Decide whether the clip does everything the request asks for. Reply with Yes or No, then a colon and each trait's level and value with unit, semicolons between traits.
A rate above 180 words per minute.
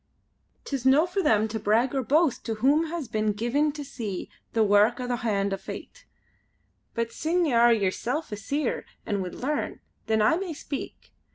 Yes: average, 190 wpm